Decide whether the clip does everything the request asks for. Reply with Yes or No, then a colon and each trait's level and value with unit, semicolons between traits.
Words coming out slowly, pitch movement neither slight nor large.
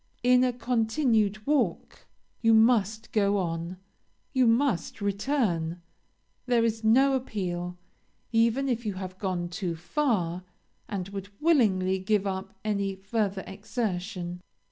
Yes: slow, 120 wpm; average, 4.0 semitones